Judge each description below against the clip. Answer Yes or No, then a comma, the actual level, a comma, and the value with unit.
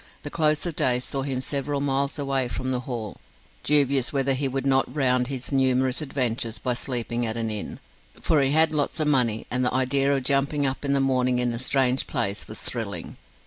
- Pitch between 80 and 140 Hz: Yes, low, 135 Hz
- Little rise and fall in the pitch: Yes, narrow, 2.0 semitones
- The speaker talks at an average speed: No, fast, 215 wpm